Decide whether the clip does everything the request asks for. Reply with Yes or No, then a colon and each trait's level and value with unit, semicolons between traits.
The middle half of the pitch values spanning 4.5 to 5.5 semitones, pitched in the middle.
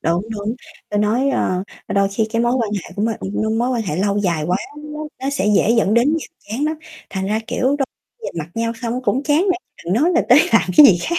No: average, 5.2 semitones; high, 225 Hz